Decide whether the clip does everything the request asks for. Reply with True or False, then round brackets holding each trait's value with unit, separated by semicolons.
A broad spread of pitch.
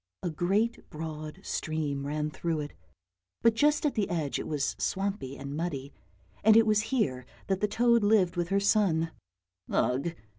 True (5.7 semitones)